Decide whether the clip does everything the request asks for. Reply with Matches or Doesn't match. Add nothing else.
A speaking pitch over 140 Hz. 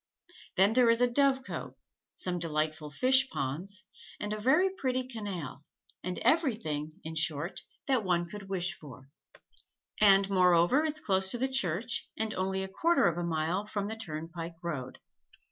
Matches